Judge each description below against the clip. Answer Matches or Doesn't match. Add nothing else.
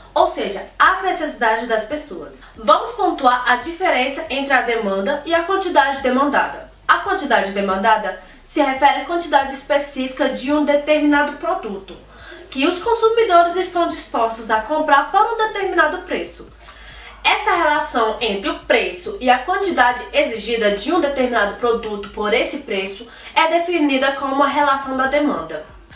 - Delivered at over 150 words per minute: Doesn't match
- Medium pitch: Doesn't match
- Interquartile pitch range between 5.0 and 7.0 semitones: Matches